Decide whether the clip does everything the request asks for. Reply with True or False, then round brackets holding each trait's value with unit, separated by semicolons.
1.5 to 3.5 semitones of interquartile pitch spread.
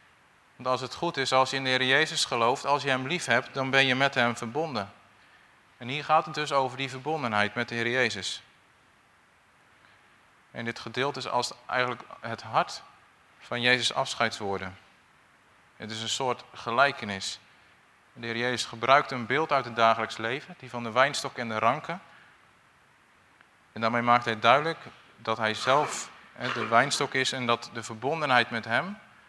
True (2.7 semitones)